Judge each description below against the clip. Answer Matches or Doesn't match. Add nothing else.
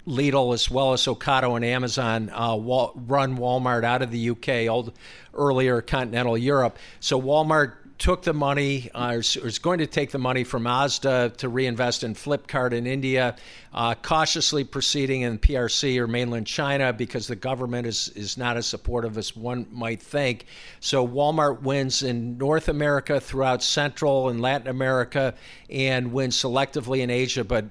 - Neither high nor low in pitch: Doesn't match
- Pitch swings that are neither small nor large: Doesn't match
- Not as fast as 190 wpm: Matches